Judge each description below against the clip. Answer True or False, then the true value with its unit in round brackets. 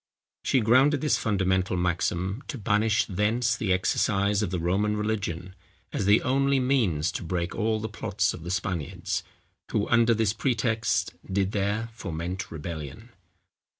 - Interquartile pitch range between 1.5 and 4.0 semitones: True (3.6 semitones)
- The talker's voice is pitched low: True (100 Hz)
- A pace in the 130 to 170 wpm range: True (150 wpm)